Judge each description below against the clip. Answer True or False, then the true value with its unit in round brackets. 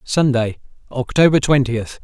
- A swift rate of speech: False (90 wpm)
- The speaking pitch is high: False (130 Hz)